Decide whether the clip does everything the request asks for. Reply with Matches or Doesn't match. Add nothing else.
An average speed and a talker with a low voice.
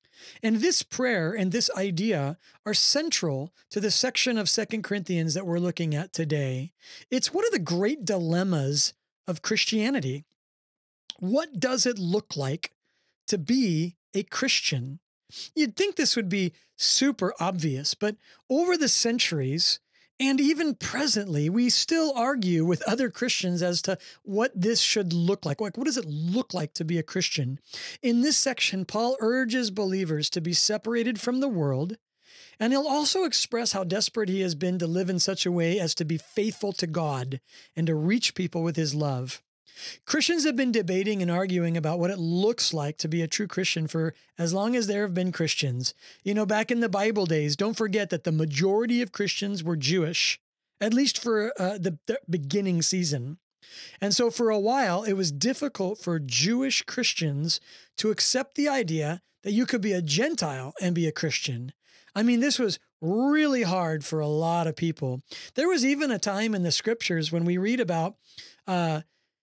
Doesn't match